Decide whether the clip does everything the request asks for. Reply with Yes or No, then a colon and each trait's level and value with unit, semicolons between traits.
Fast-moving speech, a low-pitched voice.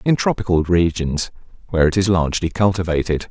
No: average, 145 wpm; very low, 90 Hz